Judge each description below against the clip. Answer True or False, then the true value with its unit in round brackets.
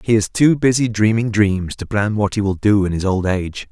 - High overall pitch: False (105 Hz)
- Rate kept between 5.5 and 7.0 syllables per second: False (5.3 syllables/s)